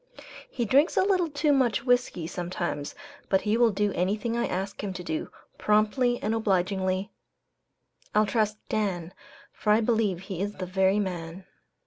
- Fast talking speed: No, average, 160 wpm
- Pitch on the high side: Yes, high, 205 Hz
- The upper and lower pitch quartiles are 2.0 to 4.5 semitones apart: Yes, average, 3.5 semitones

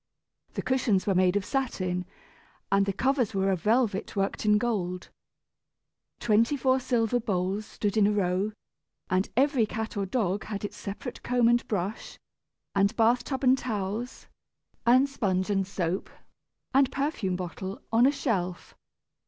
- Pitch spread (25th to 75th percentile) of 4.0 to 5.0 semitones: Yes, average, 4.3 semitones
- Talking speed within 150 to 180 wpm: Yes, average, 155 wpm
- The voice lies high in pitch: Yes, high, 210 Hz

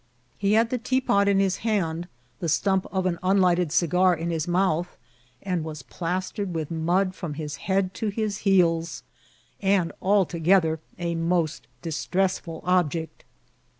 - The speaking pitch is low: No, medium, 180 Hz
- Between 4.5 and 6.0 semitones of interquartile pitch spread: No, average, 2.8 semitones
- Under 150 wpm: Yes, average, 140 wpm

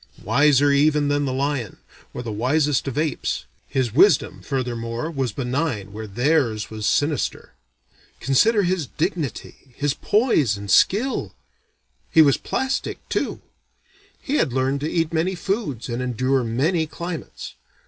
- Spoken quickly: No, average, 140 wpm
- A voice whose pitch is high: No, medium, 140 Hz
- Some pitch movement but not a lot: Yes, average, 4.6 semitones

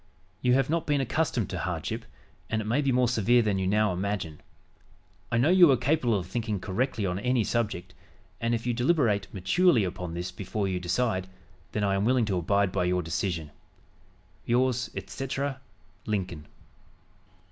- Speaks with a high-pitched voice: No, low, 110 Hz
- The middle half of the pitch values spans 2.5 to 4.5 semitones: No, average, 5.0 semitones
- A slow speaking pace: No, average, 170 wpm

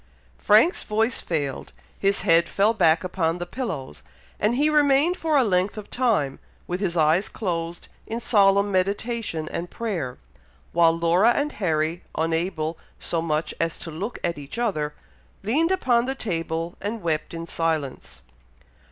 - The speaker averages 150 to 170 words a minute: Yes, average, 155 wpm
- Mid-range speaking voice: Yes, medium, 180 Hz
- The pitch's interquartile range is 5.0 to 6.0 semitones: Yes, wide, 5.5 semitones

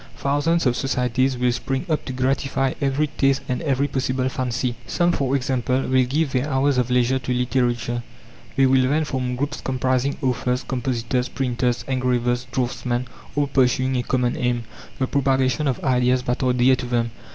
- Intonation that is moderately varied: No, narrow, 1.4 semitones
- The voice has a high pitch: No, low, 130 Hz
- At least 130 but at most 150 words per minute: No, average, 175 wpm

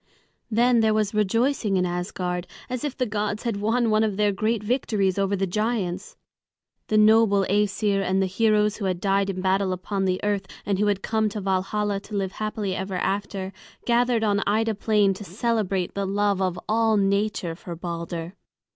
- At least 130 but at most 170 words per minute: No, average, 185 wpm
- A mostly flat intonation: Yes, narrow, 2.2 semitones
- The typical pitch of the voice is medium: No, high, 200 Hz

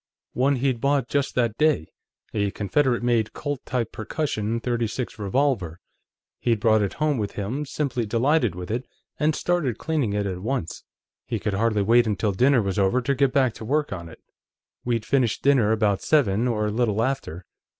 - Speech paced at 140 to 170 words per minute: No, average, 180 wpm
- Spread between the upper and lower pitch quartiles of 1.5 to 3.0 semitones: No, average, 4.6 semitones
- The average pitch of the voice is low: Yes, low, 115 Hz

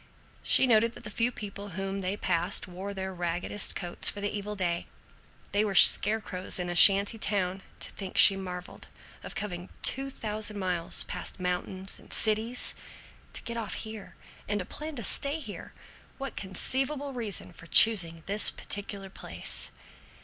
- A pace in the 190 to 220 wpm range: No, average, 165 wpm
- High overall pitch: Yes, high, 200 Hz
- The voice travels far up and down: No, average, 3.0 semitones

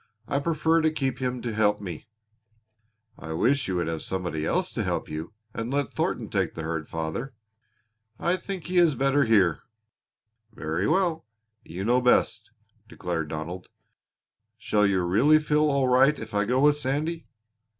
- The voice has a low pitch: Yes, low, 120 Hz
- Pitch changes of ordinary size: No, wide, 8.5 semitones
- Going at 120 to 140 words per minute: No, average, 165 wpm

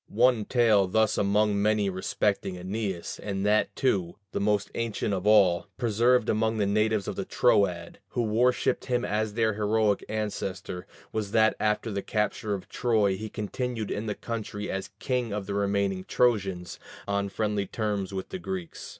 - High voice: No, low, 105 Hz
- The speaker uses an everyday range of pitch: No, narrow, 1.9 semitones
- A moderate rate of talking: Yes, average, 165 wpm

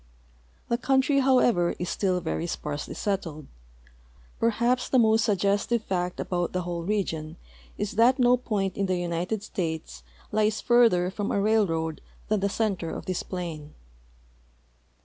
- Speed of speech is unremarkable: Yes, average, 145 wpm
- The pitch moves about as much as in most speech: Yes, average, 4.2 semitones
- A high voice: Yes, high, 195 Hz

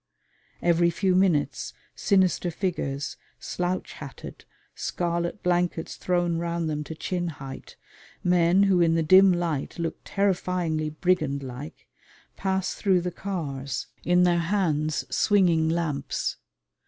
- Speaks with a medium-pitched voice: Yes, medium, 170 Hz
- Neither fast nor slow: No, slow, 120 wpm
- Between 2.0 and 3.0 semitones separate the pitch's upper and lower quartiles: Yes, narrow, 2.6 semitones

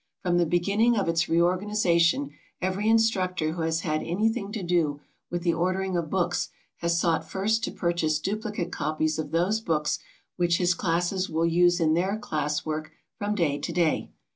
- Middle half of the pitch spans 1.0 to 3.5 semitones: Yes, average, 2.8 semitones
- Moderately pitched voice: Yes, medium, 175 Hz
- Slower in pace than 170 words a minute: No, average, 175 wpm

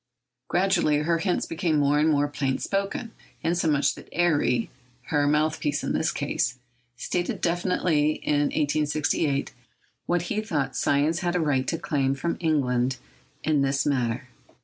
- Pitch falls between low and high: Yes, medium, 150 Hz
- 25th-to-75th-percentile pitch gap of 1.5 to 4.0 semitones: Yes, average, 3.5 semitones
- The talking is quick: No, slow, 135 wpm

